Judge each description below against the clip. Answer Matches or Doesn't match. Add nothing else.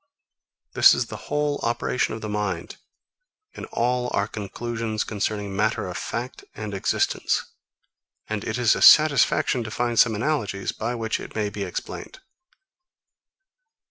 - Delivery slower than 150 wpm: Matches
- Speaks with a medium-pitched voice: Doesn't match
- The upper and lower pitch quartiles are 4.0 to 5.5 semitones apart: Doesn't match